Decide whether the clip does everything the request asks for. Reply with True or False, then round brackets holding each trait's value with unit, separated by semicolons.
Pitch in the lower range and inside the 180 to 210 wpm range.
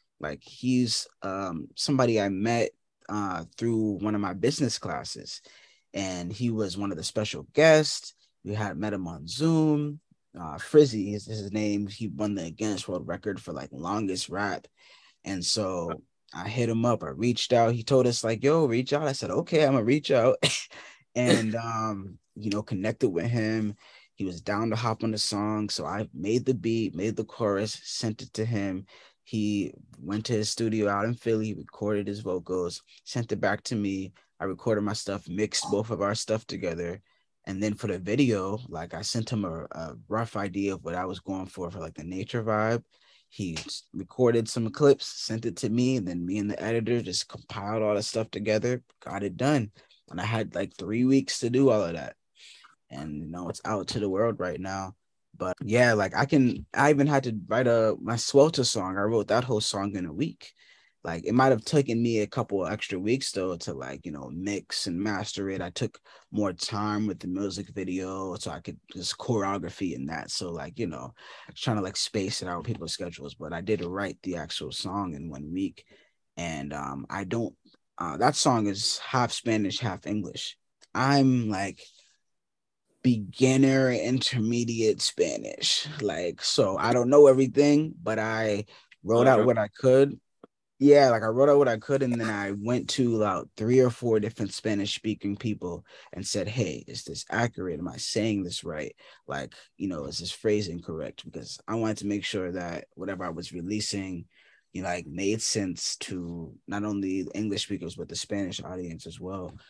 True (110 Hz; 200 wpm)